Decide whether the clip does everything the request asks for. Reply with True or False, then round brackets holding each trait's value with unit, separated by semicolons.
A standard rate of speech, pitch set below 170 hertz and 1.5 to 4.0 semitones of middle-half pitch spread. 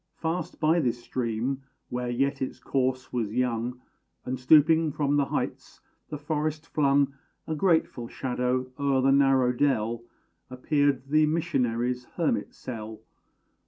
False (130 wpm; 135 Hz; 2.9 semitones)